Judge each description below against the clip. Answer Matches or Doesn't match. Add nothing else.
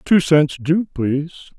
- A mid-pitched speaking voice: Matches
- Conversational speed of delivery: Matches